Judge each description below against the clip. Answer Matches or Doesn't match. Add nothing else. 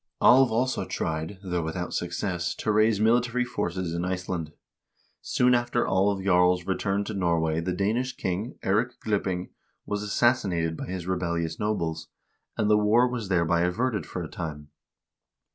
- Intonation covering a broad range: Doesn't match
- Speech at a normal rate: Matches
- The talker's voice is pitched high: Doesn't match